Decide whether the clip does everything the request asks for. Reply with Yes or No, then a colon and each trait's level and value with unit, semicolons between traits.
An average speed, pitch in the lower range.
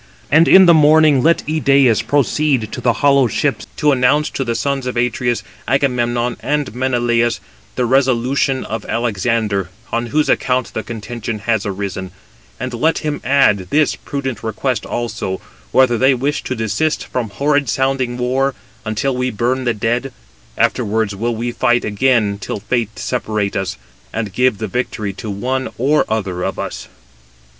Yes: average, 160 wpm; low, 120 Hz